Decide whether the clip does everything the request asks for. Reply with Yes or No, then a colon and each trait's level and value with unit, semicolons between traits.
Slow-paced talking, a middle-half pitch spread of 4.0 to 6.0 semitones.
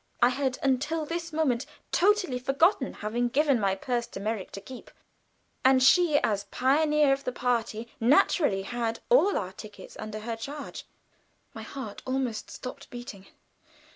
No: average, 150 wpm; average, 4.4 semitones